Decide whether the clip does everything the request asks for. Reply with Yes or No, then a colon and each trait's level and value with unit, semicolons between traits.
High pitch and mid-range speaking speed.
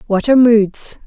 Yes: high, 225 Hz; average, 170 wpm